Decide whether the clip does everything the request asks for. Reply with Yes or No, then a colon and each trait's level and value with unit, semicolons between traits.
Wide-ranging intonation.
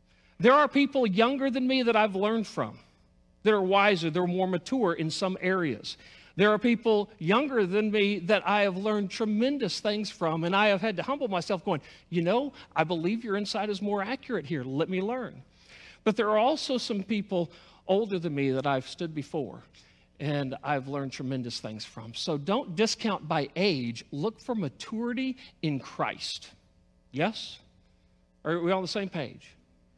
Yes: wide, 6.2 semitones